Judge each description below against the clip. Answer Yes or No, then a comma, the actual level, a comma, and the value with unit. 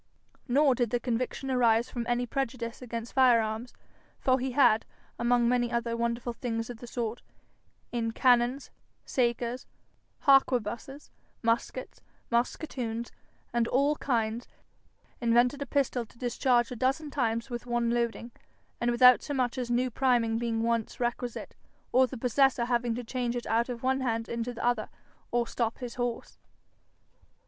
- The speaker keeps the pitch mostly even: Yes, narrow, 1.4 semitones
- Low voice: No, high, 240 Hz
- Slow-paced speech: No, average, 155 wpm